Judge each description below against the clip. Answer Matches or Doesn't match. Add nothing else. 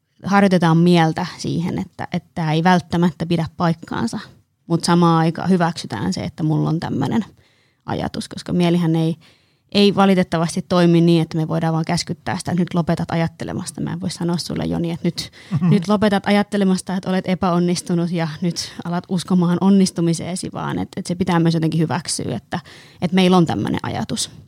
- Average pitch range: Doesn't match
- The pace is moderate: Doesn't match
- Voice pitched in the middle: Matches